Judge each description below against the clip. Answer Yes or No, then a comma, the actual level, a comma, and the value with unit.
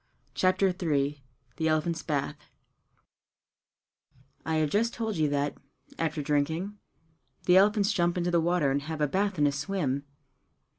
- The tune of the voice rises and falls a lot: No, average, 4.1 semitones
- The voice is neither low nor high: Yes, medium, 160 Hz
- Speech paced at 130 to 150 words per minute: Yes, average, 145 wpm